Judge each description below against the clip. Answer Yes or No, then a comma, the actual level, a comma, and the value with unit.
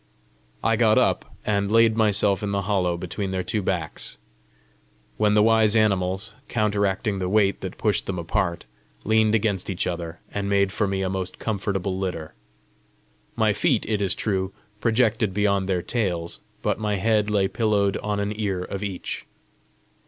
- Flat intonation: Yes, narrow, 2.1 semitones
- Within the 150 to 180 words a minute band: Yes, average, 165 wpm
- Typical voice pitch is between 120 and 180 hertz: No, low, 100 Hz